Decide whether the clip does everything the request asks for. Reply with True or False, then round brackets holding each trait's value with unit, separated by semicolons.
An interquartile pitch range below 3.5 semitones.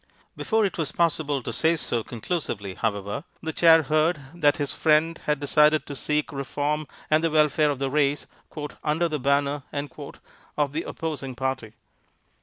True (2.4 semitones)